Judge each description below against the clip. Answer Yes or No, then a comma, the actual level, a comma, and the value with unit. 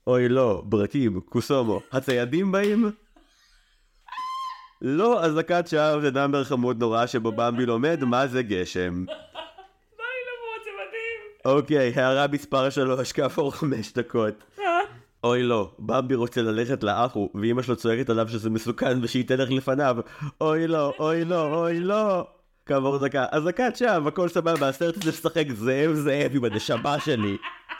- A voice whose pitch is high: No, medium, 140 Hz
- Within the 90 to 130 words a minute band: No, average, 140 wpm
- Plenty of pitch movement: Yes, wide, 6.3 semitones